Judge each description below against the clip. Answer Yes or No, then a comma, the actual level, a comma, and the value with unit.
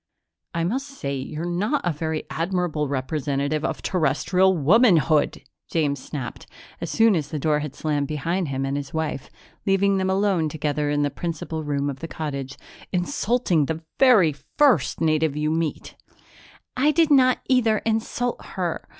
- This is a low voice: No, medium, 160 Hz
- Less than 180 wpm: Yes, average, 160 wpm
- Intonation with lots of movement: No, average, 4.8 semitones